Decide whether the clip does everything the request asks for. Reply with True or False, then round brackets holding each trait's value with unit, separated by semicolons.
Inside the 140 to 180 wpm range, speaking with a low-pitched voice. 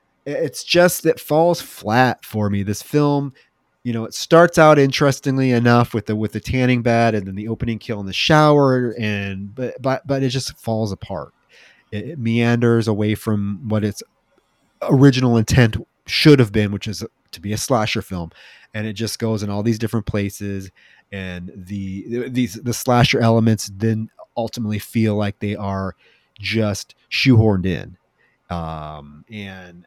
True (170 wpm; 115 Hz)